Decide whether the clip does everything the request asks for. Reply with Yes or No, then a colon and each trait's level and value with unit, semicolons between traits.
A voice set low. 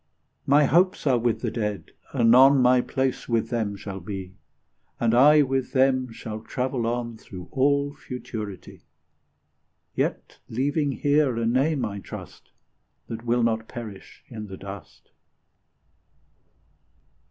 Yes: low, 120 Hz